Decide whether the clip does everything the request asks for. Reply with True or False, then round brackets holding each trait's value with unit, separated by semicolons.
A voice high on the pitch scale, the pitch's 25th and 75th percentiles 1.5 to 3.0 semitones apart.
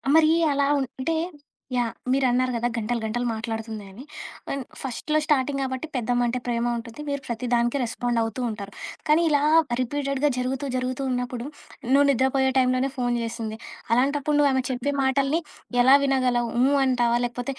True (255 Hz; 2.4 semitones)